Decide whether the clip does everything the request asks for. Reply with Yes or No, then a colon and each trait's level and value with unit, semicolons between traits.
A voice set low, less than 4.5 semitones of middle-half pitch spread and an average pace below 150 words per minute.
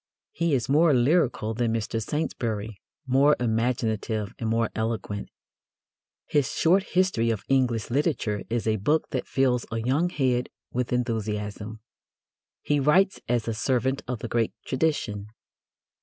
Yes: low, 120 Hz; average, 3.7 semitones; average, 140 wpm